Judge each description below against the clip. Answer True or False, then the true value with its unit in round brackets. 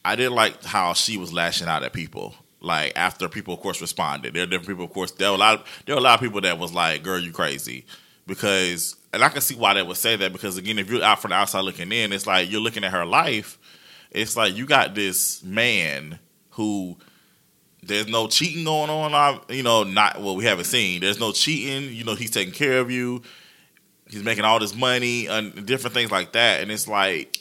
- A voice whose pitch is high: False (105 Hz)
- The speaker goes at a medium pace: False (240 wpm)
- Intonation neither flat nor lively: True (3.9 semitones)